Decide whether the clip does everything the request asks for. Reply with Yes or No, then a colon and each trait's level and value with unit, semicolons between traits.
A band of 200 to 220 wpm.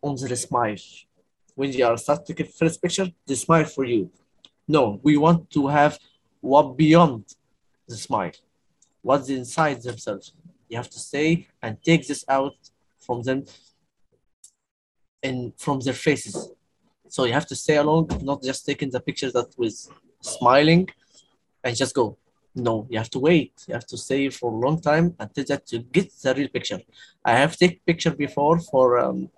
No: average, 175 wpm